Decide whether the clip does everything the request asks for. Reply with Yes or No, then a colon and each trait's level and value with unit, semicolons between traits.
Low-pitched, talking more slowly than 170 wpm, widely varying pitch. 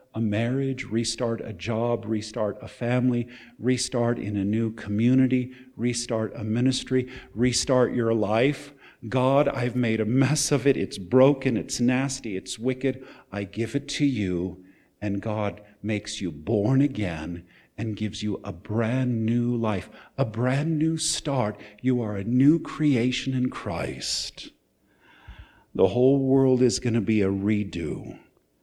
No: low, 120 Hz; average, 145 wpm; average, 3.5 semitones